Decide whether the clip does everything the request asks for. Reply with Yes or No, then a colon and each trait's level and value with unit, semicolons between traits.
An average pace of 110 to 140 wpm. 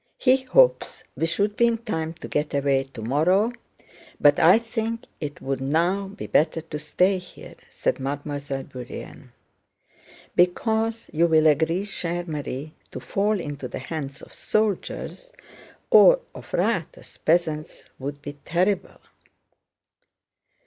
Yes: slow, 135 wpm